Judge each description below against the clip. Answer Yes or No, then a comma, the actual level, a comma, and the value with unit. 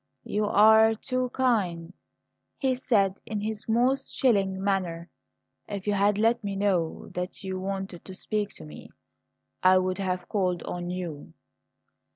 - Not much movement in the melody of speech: No, average, 3.1 semitones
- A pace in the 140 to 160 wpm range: Yes, average, 150 wpm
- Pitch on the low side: No, high, 195 Hz